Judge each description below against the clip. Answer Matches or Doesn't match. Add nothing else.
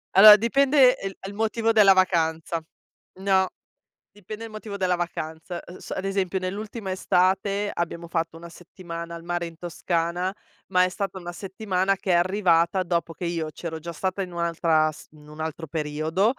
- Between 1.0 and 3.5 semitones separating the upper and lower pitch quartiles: Matches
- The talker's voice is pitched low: Doesn't match